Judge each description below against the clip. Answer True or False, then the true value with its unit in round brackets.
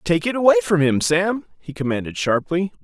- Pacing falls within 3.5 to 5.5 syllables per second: True (5.4 syllables/s)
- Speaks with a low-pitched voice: False (170 Hz)